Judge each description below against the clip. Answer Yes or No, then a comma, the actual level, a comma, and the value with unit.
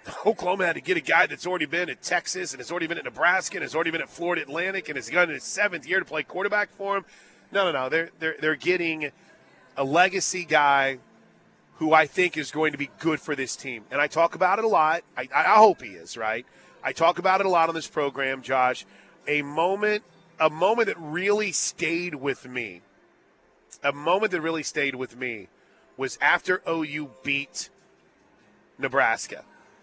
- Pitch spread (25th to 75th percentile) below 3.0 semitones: No, average, 4.2 semitones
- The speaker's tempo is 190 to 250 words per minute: Yes, average, 200 wpm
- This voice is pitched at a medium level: Yes, medium, 160 Hz